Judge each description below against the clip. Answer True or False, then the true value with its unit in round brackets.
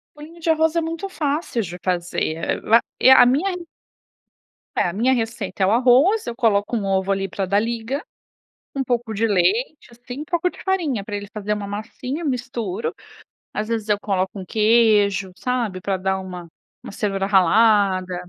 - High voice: True (225 Hz)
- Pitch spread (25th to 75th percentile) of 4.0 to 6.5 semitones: True (5.1 semitones)